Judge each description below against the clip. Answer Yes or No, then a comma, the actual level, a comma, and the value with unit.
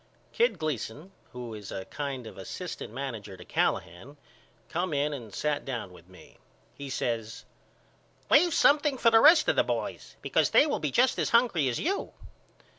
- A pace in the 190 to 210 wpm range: No, average, 175 wpm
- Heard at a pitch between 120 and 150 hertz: Yes, medium, 140 Hz